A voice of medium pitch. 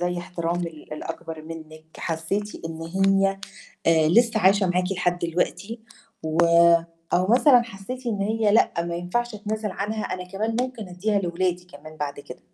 Yes: medium, 180 Hz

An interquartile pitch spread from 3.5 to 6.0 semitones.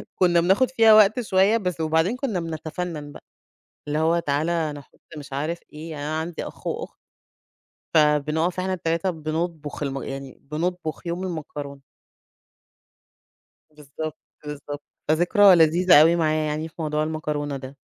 No: average, 2.8 semitones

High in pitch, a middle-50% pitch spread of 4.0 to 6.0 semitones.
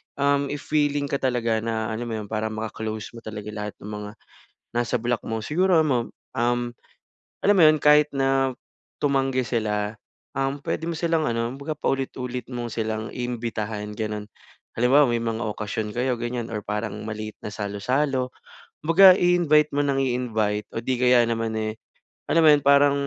No: low, 120 Hz; average, 4.3 semitones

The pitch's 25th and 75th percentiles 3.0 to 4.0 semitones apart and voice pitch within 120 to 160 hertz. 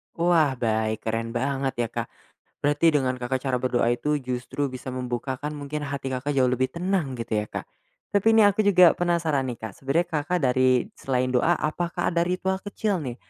No: average, 4.9 semitones; low, 135 Hz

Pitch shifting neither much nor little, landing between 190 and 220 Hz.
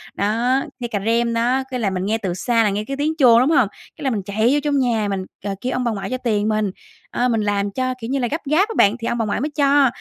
No: average, 3.8 semitones; high, 235 Hz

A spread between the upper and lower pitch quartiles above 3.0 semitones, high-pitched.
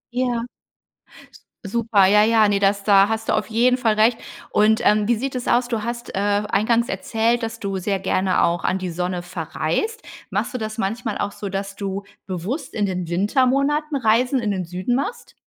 Yes: average, 3.5 semitones; high, 215 Hz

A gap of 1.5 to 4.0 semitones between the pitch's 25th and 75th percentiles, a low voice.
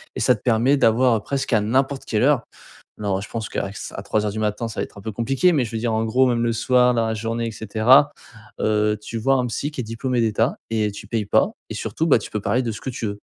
Yes: average, 2.9 semitones; low, 115 Hz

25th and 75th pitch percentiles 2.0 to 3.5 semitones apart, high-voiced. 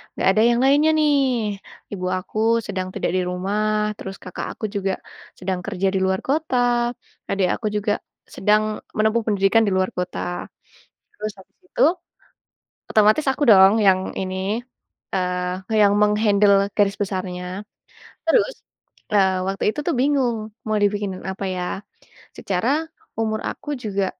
Yes: average, 3.1 semitones; high, 205 Hz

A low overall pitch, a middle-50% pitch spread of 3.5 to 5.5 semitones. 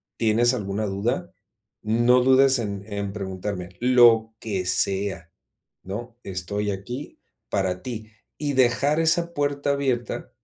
Yes: low, 115 Hz; average, 4.7 semitones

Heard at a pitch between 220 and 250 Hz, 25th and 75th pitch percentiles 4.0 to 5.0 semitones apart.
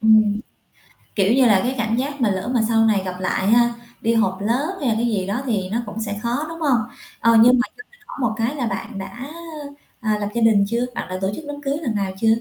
No: high, 225 Hz; average, 3.2 semitones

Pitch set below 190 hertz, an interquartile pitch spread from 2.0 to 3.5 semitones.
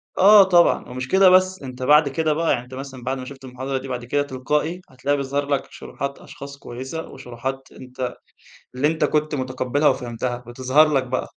Yes: low, 135 Hz; average, 2.8 semitones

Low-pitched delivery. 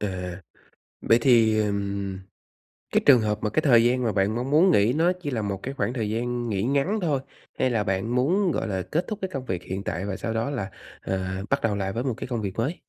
Yes: low, 115 Hz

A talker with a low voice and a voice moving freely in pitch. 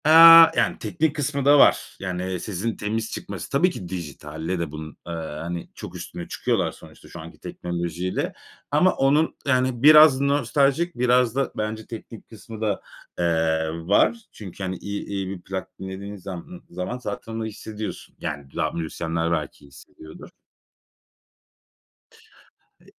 Yes: low, 100 Hz; wide, 6.9 semitones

